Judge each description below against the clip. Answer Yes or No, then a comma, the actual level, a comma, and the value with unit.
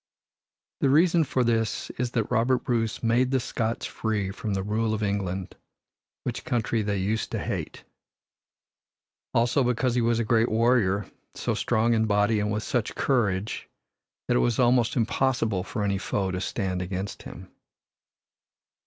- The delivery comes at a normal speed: Yes, average, 160 wpm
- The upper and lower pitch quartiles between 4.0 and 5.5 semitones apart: No, average, 3.1 semitones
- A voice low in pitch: Yes, low, 110 Hz